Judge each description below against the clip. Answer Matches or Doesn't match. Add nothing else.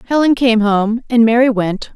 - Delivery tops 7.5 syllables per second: Doesn't match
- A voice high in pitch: Matches